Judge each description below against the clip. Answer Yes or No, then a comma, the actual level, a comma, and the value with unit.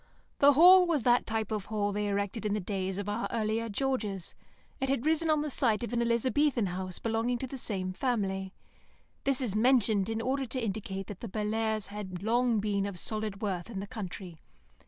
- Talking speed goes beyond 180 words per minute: Yes, average, 200 wpm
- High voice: Yes, high, 220 Hz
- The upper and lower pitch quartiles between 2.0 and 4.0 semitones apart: Yes, average, 3.7 semitones